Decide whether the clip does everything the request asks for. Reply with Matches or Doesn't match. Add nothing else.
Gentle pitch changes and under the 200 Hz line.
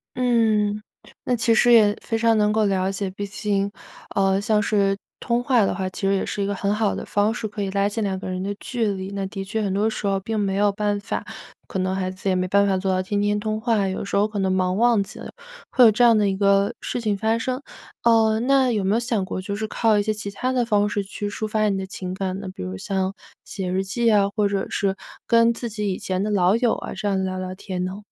Doesn't match